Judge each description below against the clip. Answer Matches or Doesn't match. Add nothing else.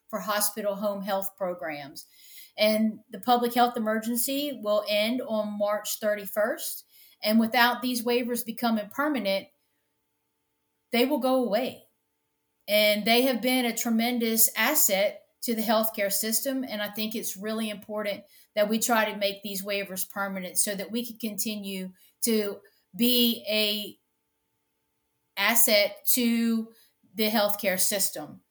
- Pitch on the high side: Matches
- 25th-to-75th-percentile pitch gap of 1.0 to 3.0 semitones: Matches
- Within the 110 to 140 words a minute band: Matches